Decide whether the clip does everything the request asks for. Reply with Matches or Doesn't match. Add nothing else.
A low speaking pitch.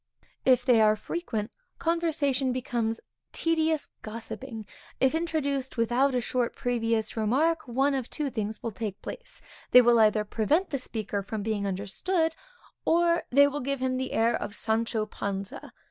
Doesn't match